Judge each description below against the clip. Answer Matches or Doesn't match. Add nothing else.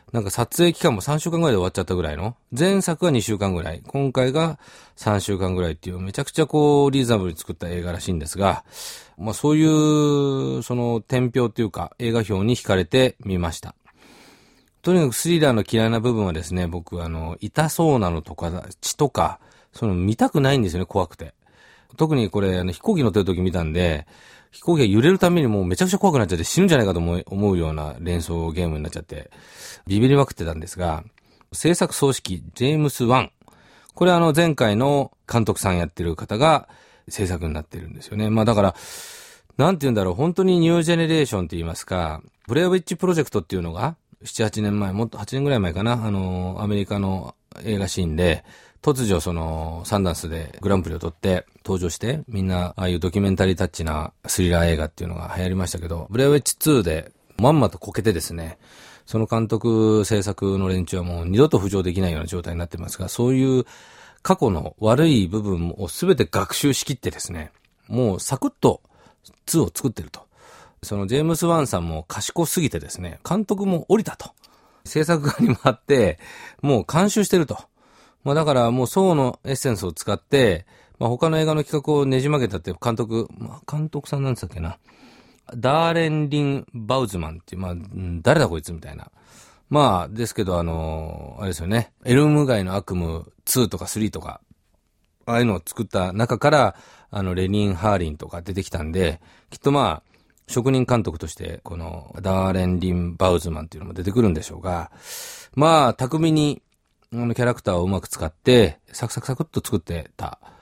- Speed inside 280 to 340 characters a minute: Doesn't match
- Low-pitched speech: Matches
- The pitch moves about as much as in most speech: Doesn't match